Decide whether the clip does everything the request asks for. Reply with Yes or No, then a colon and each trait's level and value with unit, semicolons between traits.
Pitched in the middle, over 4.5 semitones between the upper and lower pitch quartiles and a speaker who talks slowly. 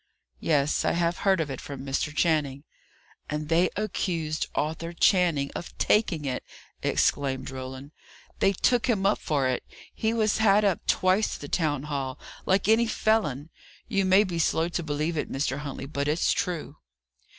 No: medium, 160 Hz; average, 4.9 semitones; average, 170 wpm